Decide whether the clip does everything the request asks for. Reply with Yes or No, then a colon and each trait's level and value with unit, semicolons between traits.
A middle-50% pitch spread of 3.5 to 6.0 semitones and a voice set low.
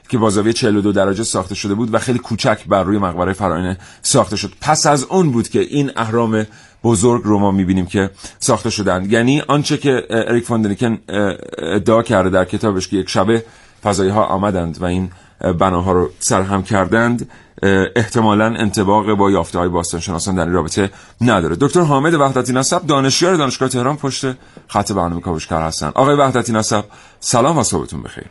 Yes: average, 4.1 semitones; low, 105 Hz